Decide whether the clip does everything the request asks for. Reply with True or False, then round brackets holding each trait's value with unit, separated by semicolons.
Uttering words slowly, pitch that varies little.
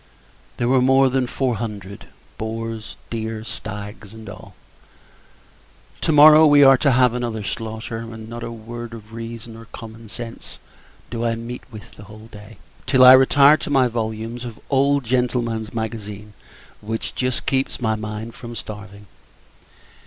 False (160 wpm; 2.3 semitones)